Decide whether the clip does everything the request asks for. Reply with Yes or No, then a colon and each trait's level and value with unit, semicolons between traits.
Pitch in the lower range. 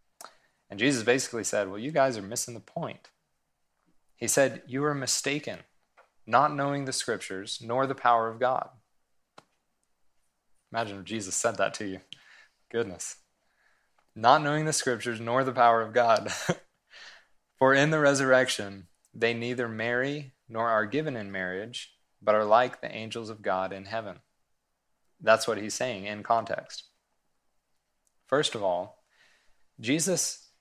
Yes: low, 115 Hz